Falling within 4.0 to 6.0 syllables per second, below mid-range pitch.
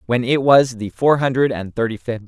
Yes: 5.6 syllables/s; low, 125 Hz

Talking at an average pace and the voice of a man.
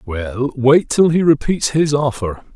Yes: average, 165 wpm; male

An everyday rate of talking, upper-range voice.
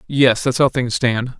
No: average, 170 wpm; low, 125 Hz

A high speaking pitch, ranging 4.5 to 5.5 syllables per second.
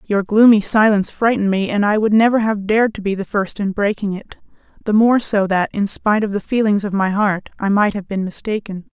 No: high, 205 Hz; 5.7 syllables/s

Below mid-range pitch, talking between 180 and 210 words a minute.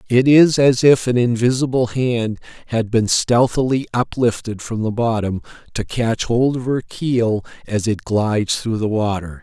No: low, 120 Hz; average, 165 wpm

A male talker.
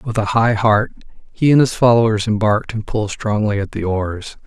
Yes: male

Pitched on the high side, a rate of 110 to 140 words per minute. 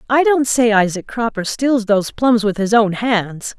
No: high, 225 Hz; average, 200 wpm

